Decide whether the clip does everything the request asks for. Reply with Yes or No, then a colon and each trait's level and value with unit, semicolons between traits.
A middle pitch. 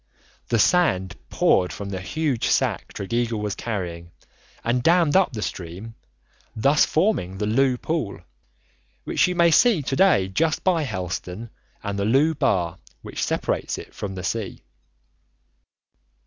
No: low, 115 Hz